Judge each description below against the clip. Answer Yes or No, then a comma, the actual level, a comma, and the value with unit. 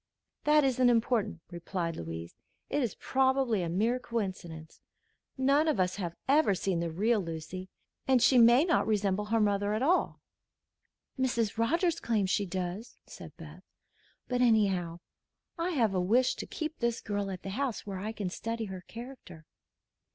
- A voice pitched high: Yes, high, 210 Hz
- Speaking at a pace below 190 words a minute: Yes, average, 165 wpm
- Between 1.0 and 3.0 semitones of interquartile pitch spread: No, average, 5.3 semitones